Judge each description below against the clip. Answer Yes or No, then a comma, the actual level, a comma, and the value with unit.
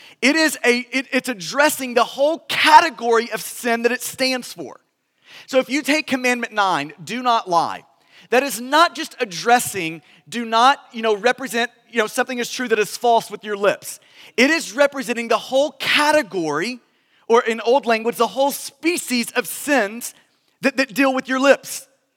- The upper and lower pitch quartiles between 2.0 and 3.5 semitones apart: Yes, average, 2.8 semitones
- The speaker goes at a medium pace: Yes, average, 180 wpm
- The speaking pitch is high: Yes, very high, 250 Hz